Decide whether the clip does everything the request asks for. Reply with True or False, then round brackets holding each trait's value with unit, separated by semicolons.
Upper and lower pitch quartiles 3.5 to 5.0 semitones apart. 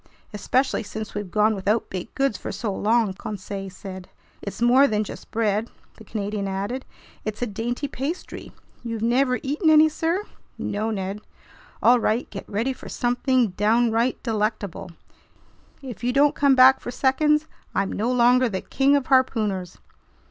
True (3.9 semitones)